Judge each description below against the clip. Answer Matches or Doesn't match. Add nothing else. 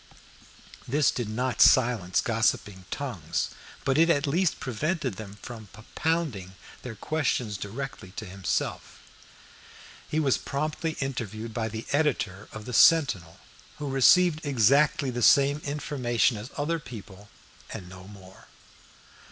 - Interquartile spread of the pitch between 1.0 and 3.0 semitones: Doesn't match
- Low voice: Matches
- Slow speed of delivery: Matches